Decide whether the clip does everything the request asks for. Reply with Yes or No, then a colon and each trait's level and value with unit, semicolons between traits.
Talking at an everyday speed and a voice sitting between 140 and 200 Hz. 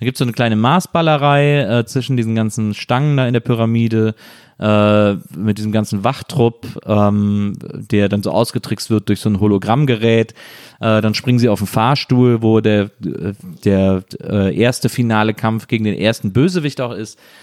No: average, 175 wpm; low, 110 Hz